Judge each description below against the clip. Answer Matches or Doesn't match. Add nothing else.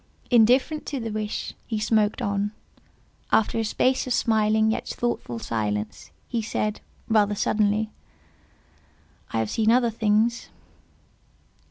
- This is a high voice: Matches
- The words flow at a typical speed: Doesn't match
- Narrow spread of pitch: Matches